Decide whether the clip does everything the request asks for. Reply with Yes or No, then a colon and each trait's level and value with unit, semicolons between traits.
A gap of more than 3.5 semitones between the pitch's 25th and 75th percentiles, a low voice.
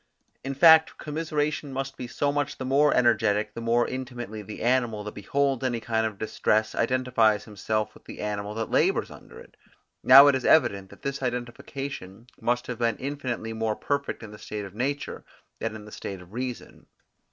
Yes: average, 3.9 semitones; low, 120 Hz